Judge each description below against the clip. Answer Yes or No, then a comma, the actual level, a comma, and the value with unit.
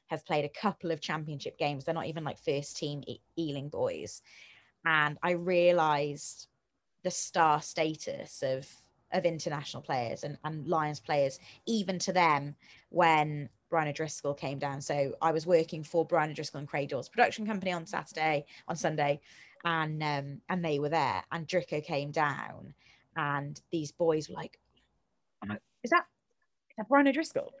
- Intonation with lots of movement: No, average, 3.1 semitones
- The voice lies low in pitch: No, medium, 155 Hz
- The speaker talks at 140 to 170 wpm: Yes, average, 165 wpm